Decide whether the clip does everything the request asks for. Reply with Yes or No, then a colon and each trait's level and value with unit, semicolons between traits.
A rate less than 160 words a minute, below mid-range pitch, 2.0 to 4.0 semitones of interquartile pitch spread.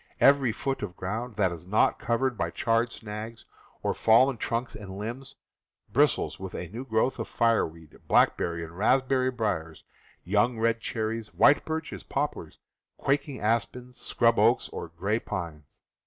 No: average, 150 wpm; low, 115 Hz; average, 4.4 semitones